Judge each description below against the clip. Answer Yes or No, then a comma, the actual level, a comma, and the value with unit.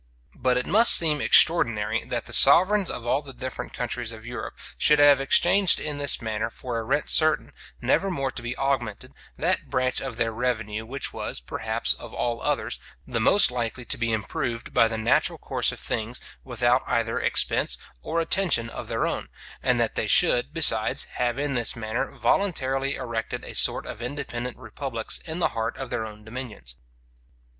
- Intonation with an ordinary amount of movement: Yes, average, 3.5 semitones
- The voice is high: No, low, 125 Hz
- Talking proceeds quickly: No, average, 185 wpm